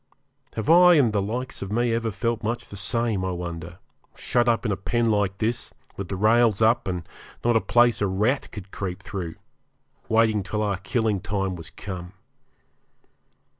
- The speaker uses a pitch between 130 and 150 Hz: No, low, 105 Hz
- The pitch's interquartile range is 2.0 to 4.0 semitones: Yes, average, 3.5 semitones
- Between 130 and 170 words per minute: No, average, 180 wpm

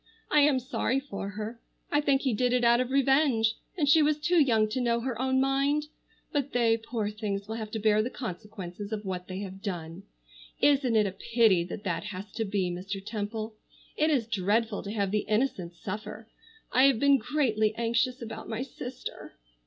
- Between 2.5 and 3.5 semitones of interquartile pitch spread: No, average, 4.2 semitones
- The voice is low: No, high, 225 Hz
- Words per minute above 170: Yes, average, 200 wpm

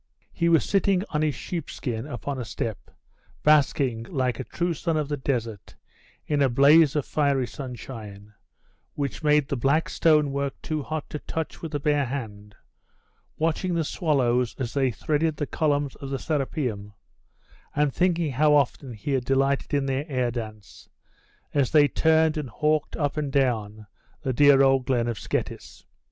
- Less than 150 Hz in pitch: Yes, medium, 140 Hz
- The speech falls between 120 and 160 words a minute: No, average, 170 wpm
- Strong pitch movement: No, average, 3.4 semitones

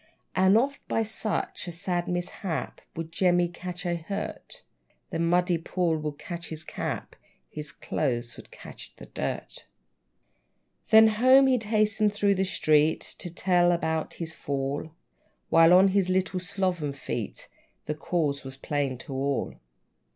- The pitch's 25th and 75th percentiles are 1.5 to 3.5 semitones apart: No, average, 3.9 semitones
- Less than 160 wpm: Yes, average, 145 wpm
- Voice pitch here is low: No, medium, 175 Hz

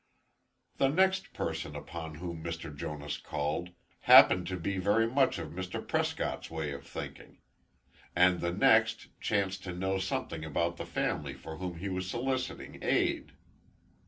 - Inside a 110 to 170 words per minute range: Yes, average, 150 wpm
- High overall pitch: No, very low, 90 Hz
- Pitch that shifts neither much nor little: Yes, average, 3.7 semitones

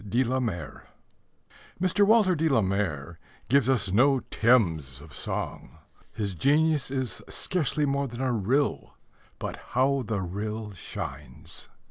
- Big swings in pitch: Yes, wide, 6.2 semitones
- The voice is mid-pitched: No, low, 120 Hz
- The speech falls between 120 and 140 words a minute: Yes, slow, 135 wpm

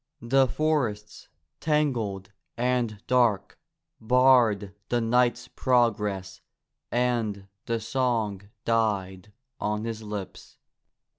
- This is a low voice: Yes, low, 115 Hz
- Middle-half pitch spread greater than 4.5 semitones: No, average, 3.2 semitones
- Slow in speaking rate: Yes, slow, 85 wpm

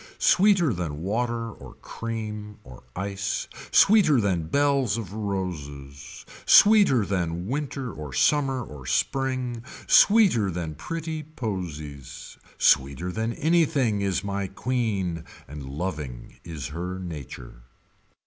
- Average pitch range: No, wide, 8.3 semitones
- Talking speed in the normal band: No, slow, 110 wpm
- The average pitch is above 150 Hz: No, low, 100 Hz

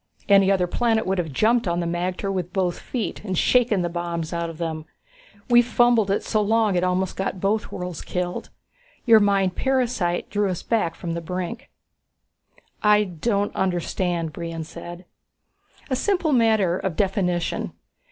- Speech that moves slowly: No, average, 160 wpm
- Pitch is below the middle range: No, high, 190 Hz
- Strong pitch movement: No, average, 3.9 semitones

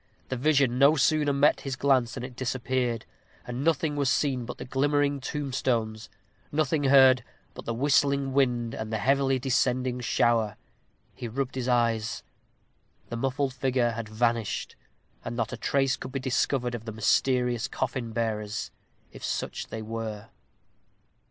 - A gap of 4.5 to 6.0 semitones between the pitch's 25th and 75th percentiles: No, average, 2.8 semitones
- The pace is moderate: Yes, average, 150 wpm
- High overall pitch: No, low, 125 Hz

